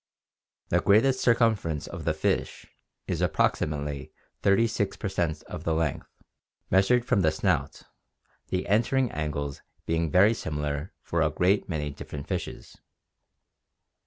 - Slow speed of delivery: Yes, slow, 130 wpm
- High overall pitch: No, very low, 85 Hz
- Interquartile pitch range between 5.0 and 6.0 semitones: Yes, wide, 5.4 semitones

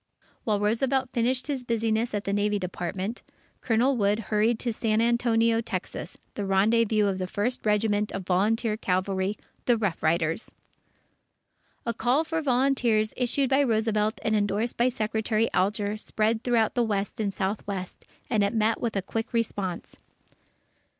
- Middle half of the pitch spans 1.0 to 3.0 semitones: Yes, narrow, 2.6 semitones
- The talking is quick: No, average, 150 wpm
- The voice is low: No, high, 220 Hz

